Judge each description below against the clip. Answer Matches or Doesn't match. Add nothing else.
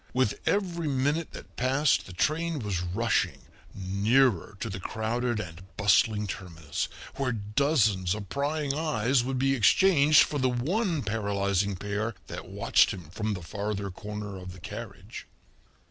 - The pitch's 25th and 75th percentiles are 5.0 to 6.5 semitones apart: Matches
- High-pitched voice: Doesn't match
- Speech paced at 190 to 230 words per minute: Doesn't match